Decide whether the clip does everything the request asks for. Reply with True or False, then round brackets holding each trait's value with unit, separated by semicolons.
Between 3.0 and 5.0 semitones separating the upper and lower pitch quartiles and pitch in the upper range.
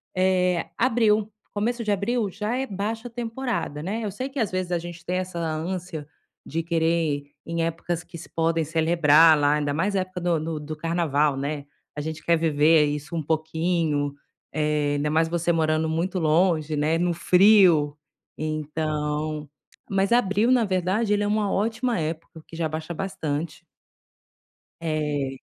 False (3.8 semitones; 165 Hz)